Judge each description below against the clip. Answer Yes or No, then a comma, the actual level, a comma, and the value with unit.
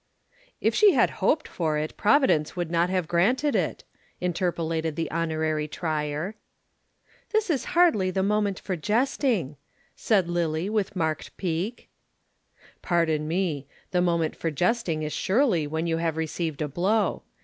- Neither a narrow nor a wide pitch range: Yes, average, 4.3 semitones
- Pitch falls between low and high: Yes, medium, 170 Hz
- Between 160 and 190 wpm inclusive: No, average, 145 wpm